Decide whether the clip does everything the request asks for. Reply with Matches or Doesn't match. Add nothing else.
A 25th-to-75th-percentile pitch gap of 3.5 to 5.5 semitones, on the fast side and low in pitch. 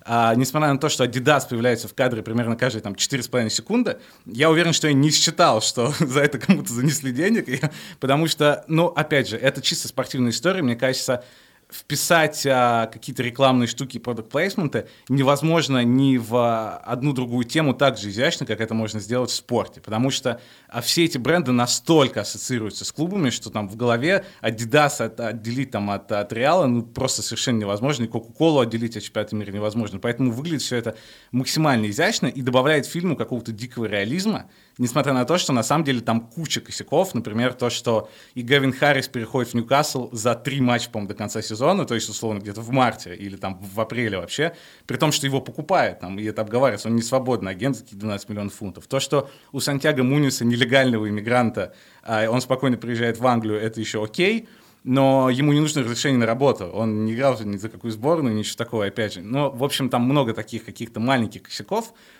Matches